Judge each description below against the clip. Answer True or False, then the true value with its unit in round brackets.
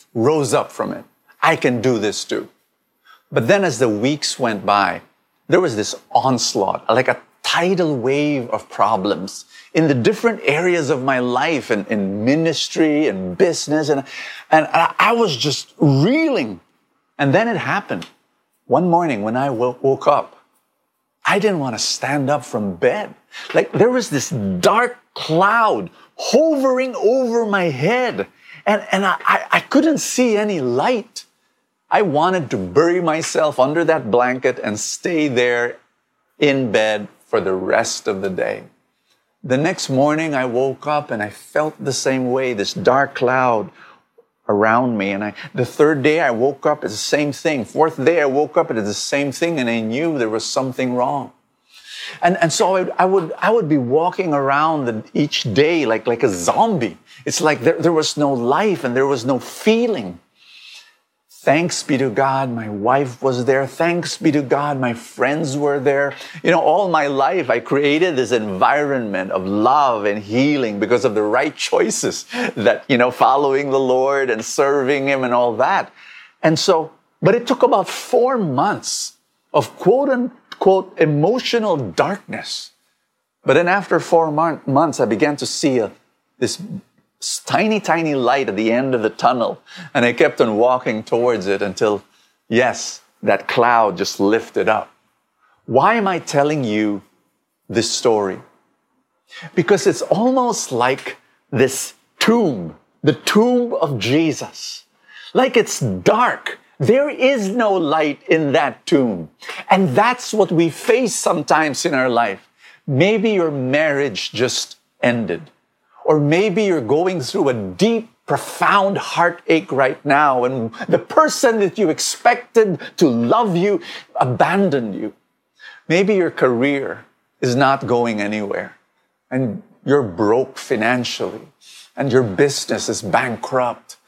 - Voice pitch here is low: False (145 Hz)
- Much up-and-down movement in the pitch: True (6.1 semitones)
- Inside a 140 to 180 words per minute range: True (160 wpm)